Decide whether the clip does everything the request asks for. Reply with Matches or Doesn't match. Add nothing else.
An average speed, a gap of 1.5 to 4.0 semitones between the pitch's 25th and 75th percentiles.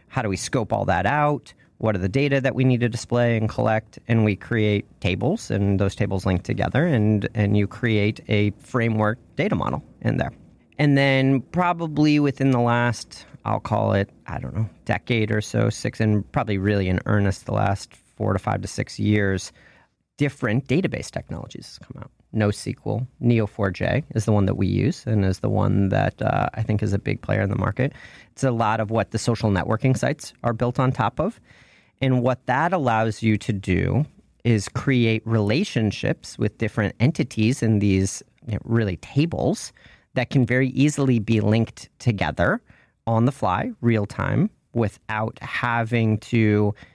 Matches